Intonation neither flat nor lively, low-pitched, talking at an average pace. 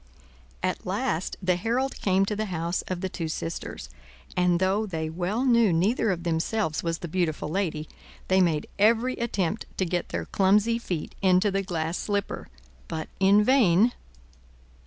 No: average, 3.6 semitones; medium, 185 Hz; average, 160 wpm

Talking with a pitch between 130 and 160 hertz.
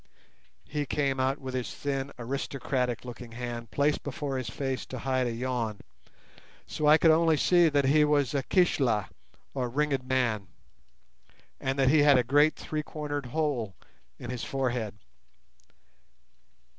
Yes: low, 135 Hz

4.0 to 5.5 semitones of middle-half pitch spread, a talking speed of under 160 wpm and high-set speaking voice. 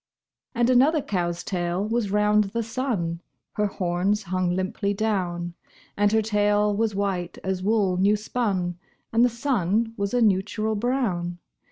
No: average, 3.2 semitones; average, 150 wpm; high, 205 Hz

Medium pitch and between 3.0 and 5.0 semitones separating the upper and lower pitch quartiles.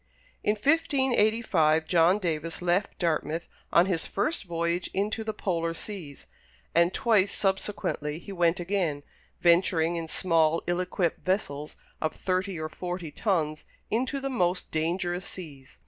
Yes: medium, 175 Hz; average, 3.4 semitones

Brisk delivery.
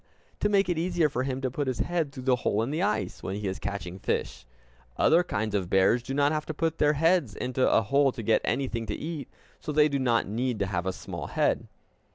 Yes: fast, 245 wpm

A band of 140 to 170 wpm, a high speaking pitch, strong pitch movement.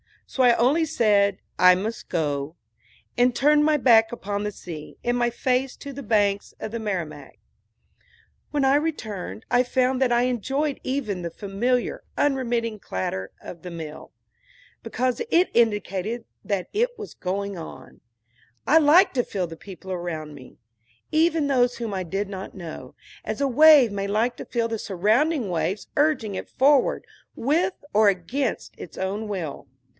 Yes: average, 160 wpm; high, 225 Hz; wide, 5.7 semitones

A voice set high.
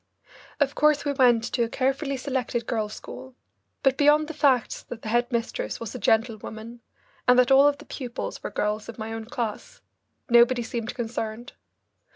Yes: high, 240 Hz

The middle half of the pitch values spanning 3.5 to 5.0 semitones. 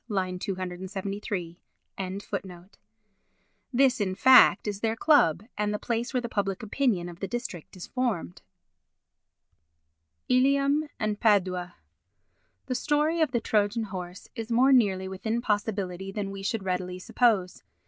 Yes: average, 4.4 semitones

